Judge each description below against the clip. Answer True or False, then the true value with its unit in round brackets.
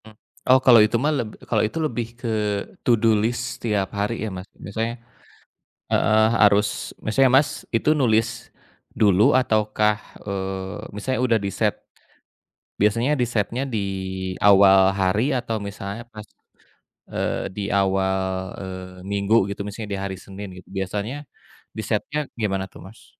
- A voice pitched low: True (105 Hz)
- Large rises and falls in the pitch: False (3.0 semitones)